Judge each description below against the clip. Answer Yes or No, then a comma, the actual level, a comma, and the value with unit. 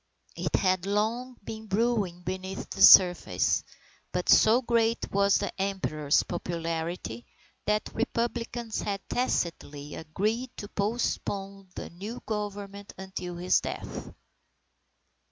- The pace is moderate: No, slow, 110 wpm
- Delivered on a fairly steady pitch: No, average, 3.7 semitones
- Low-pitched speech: No, high, 200 Hz